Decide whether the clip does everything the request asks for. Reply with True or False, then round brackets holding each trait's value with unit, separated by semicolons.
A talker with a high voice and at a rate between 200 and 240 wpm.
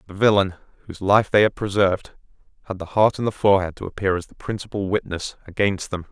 False (100 Hz; 205 wpm)